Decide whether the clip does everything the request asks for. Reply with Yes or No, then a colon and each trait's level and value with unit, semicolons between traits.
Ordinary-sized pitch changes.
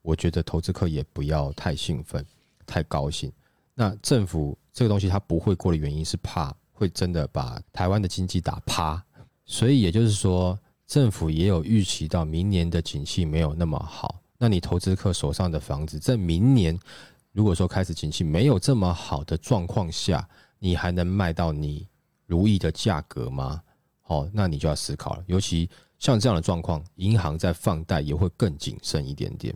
Yes: average, 4.0 semitones